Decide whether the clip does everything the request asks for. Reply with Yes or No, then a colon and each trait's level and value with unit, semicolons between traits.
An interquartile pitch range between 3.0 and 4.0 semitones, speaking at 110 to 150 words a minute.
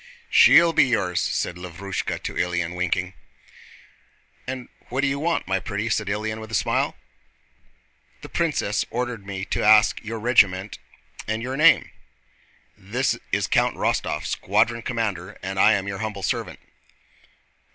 Yes: average, 3.5 semitones; average, 140 wpm